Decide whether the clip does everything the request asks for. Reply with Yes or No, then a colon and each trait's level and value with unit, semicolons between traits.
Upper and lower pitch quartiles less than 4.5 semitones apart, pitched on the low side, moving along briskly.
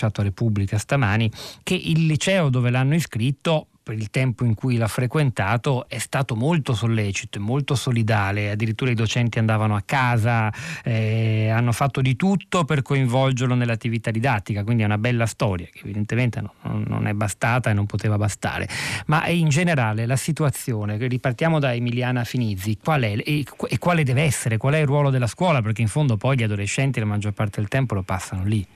Yes: average, 4.1 semitones; low, 120 Hz; fast, 185 wpm